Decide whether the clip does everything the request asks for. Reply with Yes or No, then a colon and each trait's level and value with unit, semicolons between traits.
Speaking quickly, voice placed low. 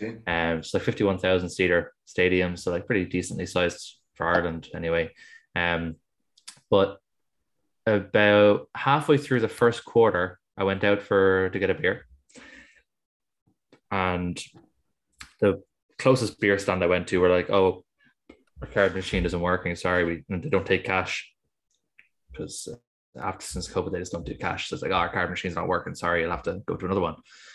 No: average, 175 wpm; very low, 90 Hz